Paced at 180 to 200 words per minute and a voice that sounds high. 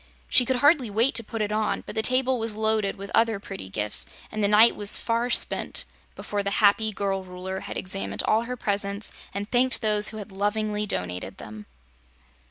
Yes: average, 195 wpm; high, 210 Hz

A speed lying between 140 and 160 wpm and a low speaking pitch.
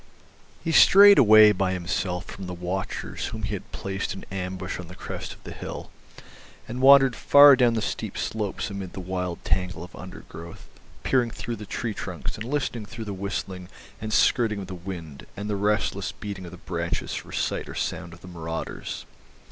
No: average, 190 wpm; very low, 95 Hz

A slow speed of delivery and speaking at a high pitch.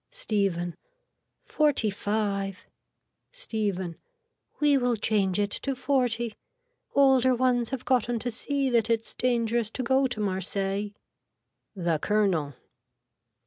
Yes: slow, 110 wpm; high, 225 Hz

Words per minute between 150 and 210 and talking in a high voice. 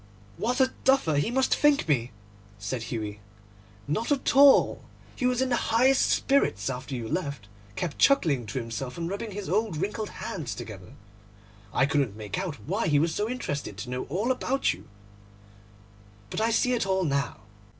No: average, 175 wpm; medium, 170 Hz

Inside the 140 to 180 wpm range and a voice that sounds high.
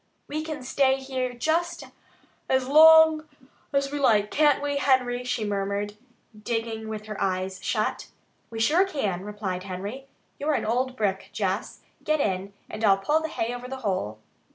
Yes: average, 165 wpm; high, 245 Hz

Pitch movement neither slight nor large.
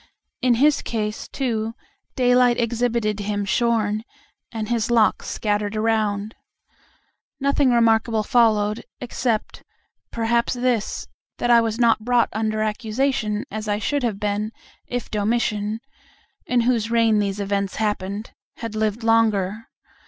No: narrow, 2.1 semitones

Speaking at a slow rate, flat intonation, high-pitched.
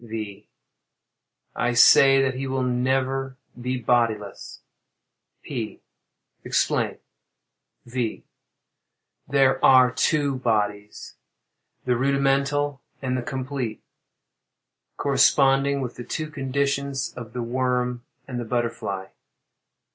No: slow, 95 wpm; narrow, 2.2 semitones; low, 130 Hz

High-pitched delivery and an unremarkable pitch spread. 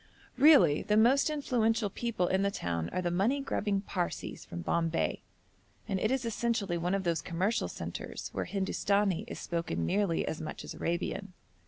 Yes: high, 195 Hz; average, 4.9 semitones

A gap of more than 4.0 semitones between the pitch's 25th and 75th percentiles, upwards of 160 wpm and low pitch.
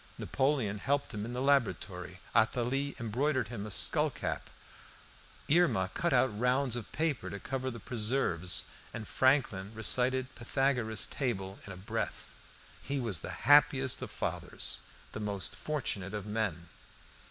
No: average, 4.7 semitones; average, 140 wpm; low, 120 Hz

